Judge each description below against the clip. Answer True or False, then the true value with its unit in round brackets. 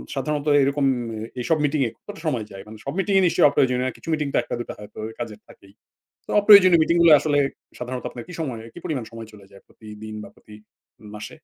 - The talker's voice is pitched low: True (130 Hz)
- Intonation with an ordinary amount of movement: False (6.1 semitones)